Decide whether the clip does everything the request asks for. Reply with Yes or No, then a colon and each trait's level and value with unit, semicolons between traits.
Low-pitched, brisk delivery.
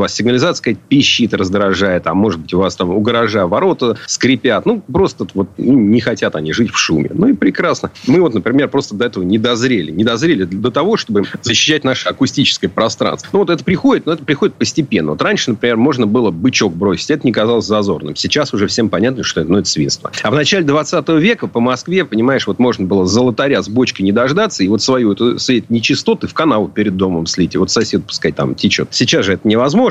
Yes: low, 120 Hz; fast, 215 wpm